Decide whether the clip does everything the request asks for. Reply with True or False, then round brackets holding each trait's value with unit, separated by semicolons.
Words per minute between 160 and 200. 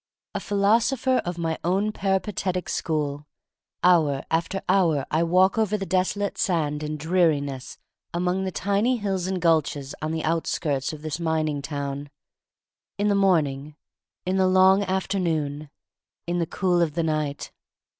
False (145 wpm)